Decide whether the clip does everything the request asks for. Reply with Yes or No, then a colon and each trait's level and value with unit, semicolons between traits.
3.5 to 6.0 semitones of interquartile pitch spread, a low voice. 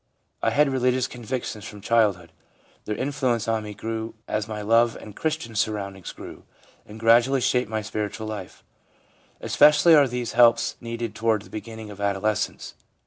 No: narrow, 2.6 semitones; low, 115 Hz